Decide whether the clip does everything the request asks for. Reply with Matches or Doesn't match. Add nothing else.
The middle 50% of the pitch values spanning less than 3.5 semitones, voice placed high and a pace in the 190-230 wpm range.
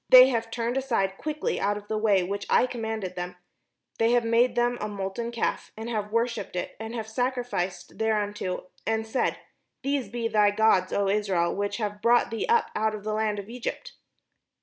Matches